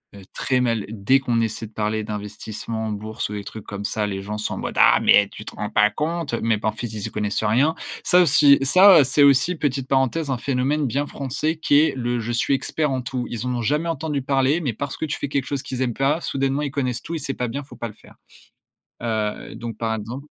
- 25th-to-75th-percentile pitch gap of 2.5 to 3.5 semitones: No, average, 4.5 semitones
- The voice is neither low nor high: No, low, 125 Hz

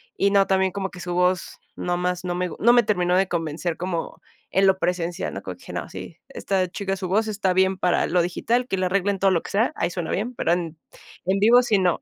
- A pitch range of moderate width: No, narrow, 1.9 semitones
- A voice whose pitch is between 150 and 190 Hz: Yes, medium, 185 Hz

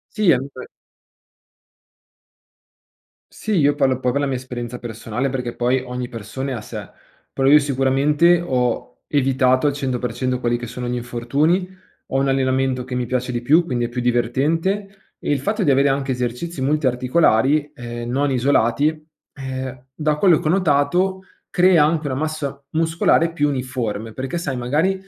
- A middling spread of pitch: Yes, average, 3.5 semitones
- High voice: No, low, 135 Hz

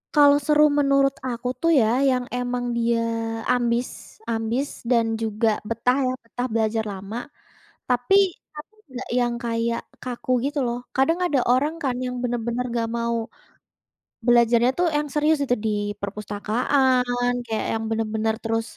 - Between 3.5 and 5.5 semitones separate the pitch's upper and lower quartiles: No, narrow, 2.5 semitones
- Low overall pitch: No, high, 245 Hz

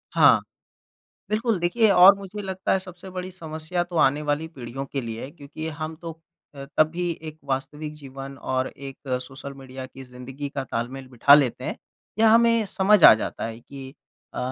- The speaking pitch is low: No, medium, 150 Hz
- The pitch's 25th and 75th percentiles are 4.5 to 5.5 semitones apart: Yes, average, 5.1 semitones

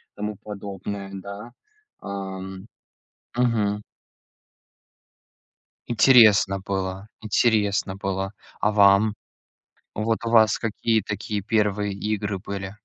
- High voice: No, low, 100 Hz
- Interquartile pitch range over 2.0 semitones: No, narrow, 1.7 semitones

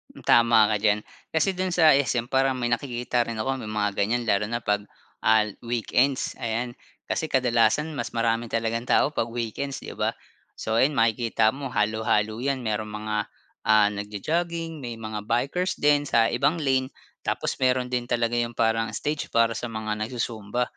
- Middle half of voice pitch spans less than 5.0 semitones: Yes, average, 3.3 semitones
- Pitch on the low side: Yes, low, 120 Hz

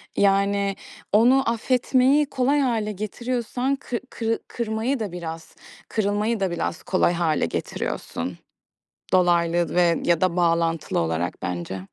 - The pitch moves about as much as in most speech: No, wide, 5.7 semitones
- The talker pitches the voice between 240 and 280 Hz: No, high, 200 Hz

